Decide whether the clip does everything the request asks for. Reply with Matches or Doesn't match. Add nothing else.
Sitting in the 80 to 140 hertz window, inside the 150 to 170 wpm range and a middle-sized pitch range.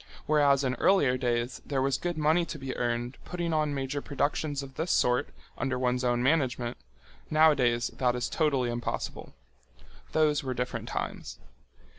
Matches